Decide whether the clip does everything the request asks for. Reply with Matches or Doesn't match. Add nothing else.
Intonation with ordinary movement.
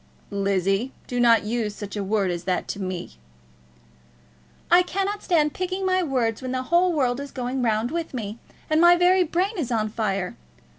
Doesn't match